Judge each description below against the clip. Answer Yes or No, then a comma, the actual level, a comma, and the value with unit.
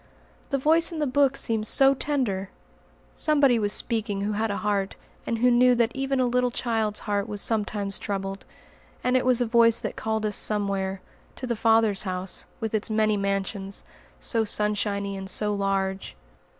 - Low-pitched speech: No, high, 215 Hz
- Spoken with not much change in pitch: No, average, 3.6 semitones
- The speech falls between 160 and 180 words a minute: Yes, average, 175 wpm